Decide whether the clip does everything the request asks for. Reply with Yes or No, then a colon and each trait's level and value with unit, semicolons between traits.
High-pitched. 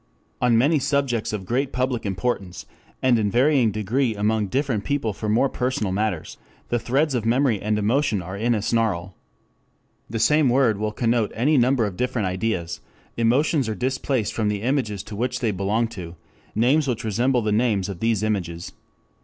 No: low, 115 Hz